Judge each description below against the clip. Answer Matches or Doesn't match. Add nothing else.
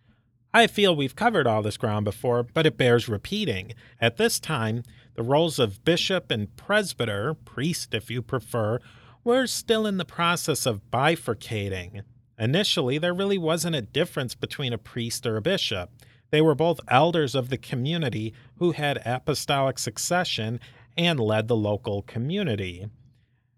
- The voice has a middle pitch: Doesn't match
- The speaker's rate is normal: Matches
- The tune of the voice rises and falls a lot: Matches